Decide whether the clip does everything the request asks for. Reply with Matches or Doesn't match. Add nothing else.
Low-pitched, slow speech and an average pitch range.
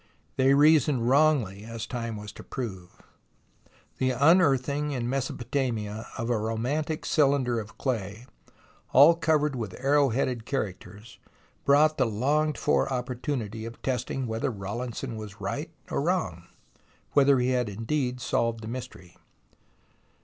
Matches